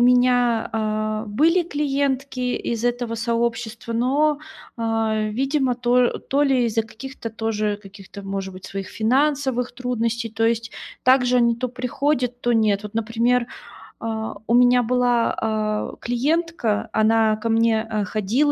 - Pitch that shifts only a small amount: Yes, narrow, 2.3 semitones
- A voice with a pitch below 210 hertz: No, high, 235 Hz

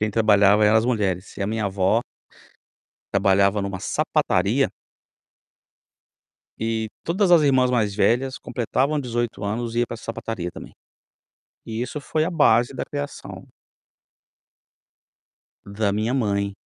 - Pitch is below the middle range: Yes, low, 110 Hz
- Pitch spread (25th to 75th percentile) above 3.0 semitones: Yes, average, 3.8 semitones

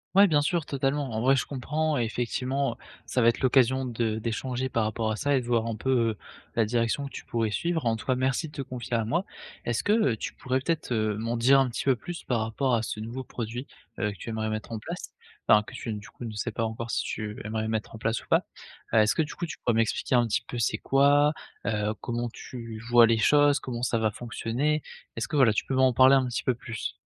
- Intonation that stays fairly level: No, average, 3.1 semitones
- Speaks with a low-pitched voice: Yes, low, 120 Hz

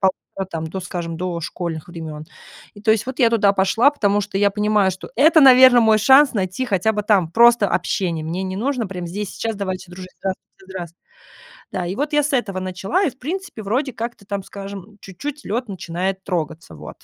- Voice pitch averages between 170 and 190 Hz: No, high, 200 Hz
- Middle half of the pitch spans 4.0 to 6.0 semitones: Yes, average, 4.3 semitones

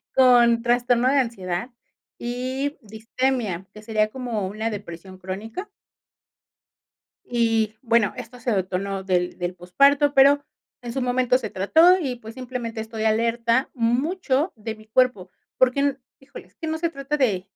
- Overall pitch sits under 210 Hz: No, high, 235 Hz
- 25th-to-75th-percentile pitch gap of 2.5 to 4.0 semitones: Yes, average, 3.6 semitones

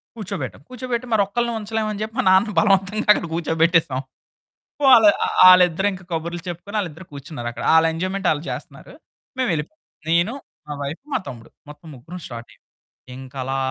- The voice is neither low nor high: Yes, medium, 180 Hz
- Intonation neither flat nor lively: Yes, average, 4.9 semitones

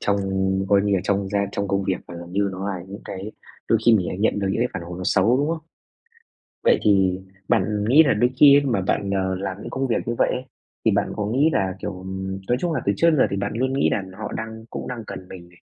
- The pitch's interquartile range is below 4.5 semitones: Yes, average, 3.8 semitones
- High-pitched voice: No, low, 100 Hz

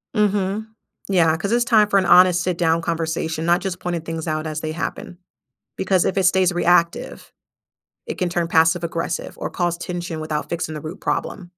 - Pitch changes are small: Yes, narrow, 2.3 semitones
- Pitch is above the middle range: No, medium, 175 Hz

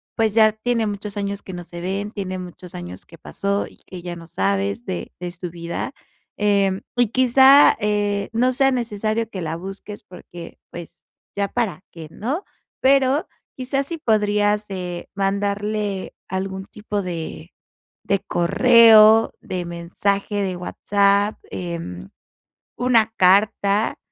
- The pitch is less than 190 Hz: No, high, 200 Hz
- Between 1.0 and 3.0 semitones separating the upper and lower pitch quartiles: No, average, 3.4 semitones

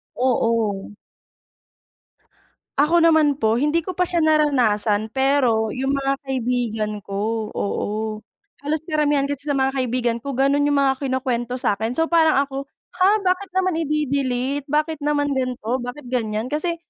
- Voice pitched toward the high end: Yes, very high, 270 Hz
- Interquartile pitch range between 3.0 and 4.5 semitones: Yes, average, 3.8 semitones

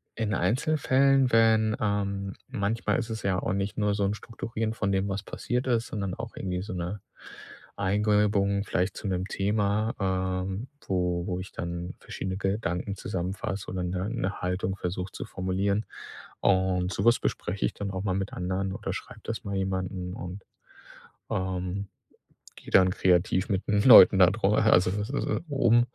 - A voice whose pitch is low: Yes, low, 100 Hz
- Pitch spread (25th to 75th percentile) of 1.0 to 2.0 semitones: No, narrow, 2.5 semitones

